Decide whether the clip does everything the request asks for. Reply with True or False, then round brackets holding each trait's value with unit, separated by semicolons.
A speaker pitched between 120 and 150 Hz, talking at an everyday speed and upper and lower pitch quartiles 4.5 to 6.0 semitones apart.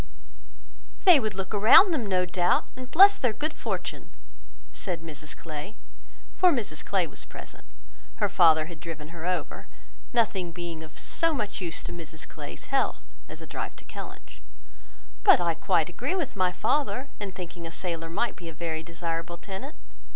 False (180 Hz; 175 wpm; 5.1 semitones)